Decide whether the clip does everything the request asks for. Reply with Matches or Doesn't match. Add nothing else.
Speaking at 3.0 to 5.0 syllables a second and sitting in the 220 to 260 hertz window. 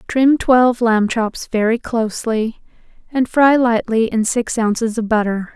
Matches